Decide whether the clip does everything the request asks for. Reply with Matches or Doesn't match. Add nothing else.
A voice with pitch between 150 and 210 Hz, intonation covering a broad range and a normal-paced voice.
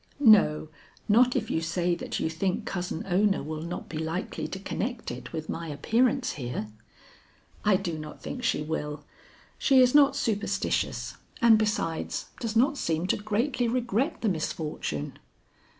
Matches